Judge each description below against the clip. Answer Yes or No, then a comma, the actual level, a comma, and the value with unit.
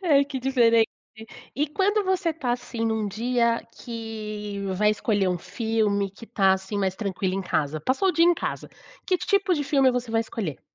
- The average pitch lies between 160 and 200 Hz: No, high, 230 Hz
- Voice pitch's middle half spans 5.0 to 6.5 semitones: Yes, average, 5.3 semitones